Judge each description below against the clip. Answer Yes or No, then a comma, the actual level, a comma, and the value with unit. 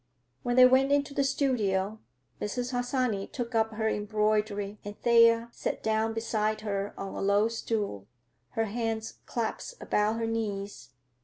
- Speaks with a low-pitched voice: No, high, 220 Hz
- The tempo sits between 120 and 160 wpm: Yes, average, 150 wpm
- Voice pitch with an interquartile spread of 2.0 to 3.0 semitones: Yes, narrow, 2.4 semitones